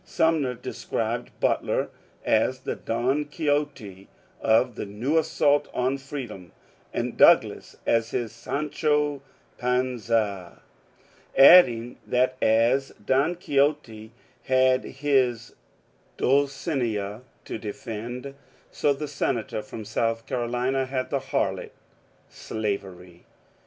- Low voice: Yes, low, 125 Hz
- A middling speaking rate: No, slow, 105 wpm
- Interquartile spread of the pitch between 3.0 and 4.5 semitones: Yes, average, 3.8 semitones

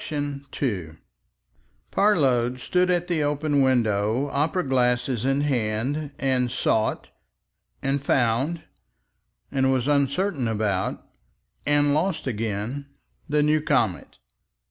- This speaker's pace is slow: Yes, slow, 105 wpm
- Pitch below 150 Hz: Yes, low, 135 Hz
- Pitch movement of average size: Yes, average, 3.6 semitones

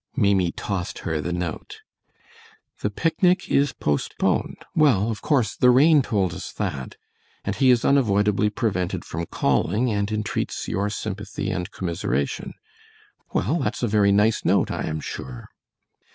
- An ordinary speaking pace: Yes, average, 145 wpm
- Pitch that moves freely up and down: Yes, wide, 5.7 semitones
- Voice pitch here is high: No, low, 105 Hz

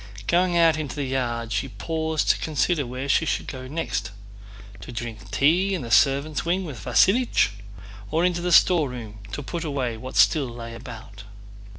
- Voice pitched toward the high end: No, low, 135 Hz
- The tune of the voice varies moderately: No, wide, 5.9 semitones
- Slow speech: No, average, 170 wpm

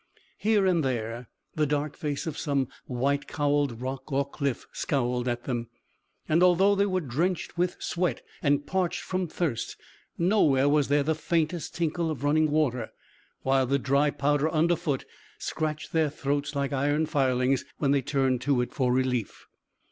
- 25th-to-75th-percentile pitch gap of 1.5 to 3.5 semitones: Yes, average, 3.2 semitones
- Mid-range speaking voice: Yes, medium, 145 Hz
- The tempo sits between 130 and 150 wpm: No, average, 165 wpm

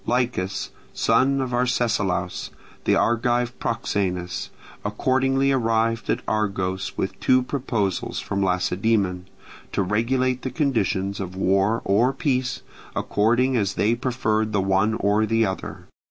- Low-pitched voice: Yes, low, 110 Hz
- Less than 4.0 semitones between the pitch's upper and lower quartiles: No, average, 4.4 semitones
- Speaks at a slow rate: Yes, slow, 125 wpm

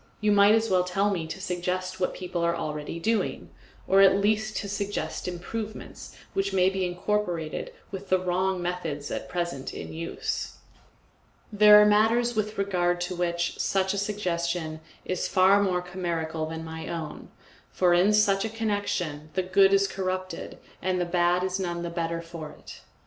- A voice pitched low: No, medium, 185 Hz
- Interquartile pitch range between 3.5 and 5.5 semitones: No, average, 2.7 semitones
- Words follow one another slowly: No, average, 170 wpm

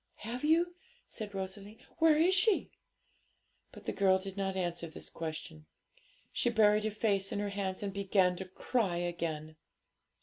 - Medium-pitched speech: No, high, 195 Hz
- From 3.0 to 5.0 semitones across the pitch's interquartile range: Yes, average, 3.3 semitones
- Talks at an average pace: Yes, average, 160 wpm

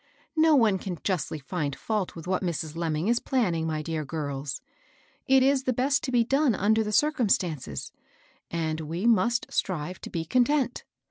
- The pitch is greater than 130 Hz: Yes, medium, 185 Hz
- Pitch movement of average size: No, wide, 7.2 semitones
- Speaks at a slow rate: No, average, 180 wpm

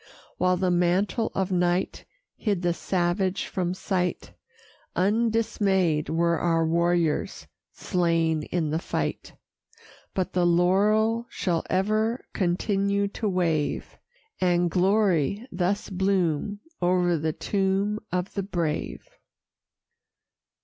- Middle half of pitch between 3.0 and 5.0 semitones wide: No, narrow, 2.5 semitones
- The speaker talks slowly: Yes, slow, 105 wpm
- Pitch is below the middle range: No, medium, 180 Hz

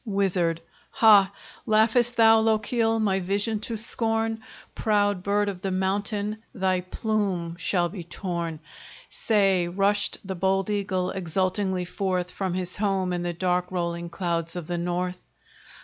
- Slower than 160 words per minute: Yes, average, 140 wpm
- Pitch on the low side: No, high, 190 Hz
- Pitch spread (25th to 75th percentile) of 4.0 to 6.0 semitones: No, average, 2.7 semitones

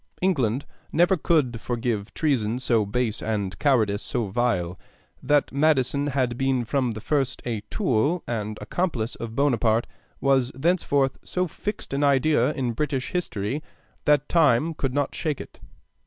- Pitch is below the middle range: Yes, low, 130 Hz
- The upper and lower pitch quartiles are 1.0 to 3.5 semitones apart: No, average, 4.3 semitones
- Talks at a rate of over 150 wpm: No, average, 145 wpm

